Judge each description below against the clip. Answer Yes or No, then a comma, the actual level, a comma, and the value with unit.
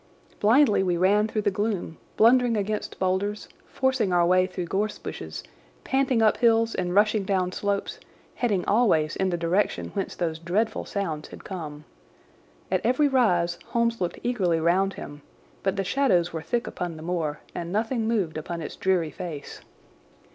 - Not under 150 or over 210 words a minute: Yes, average, 165 wpm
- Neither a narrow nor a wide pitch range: Yes, average, 4.3 semitones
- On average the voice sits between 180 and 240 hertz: Yes, high, 190 Hz